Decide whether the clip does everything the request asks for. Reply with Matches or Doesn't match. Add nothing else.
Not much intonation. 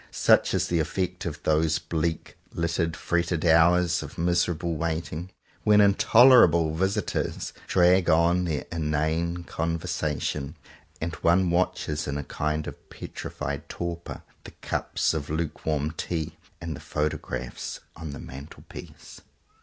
Matches